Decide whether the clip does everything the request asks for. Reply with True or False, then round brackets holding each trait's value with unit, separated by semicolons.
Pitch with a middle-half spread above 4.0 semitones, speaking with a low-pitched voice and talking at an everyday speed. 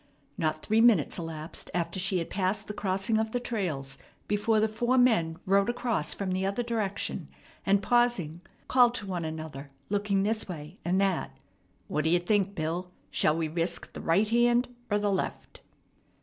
False (4.7 semitones; 195 Hz; 175 wpm)